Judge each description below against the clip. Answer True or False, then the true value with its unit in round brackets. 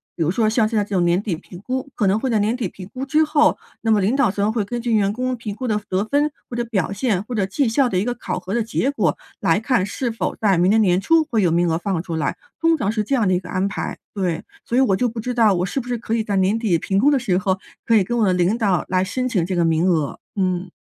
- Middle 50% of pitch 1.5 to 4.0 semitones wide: False (4.4 semitones)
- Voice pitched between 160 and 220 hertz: True (210 Hz)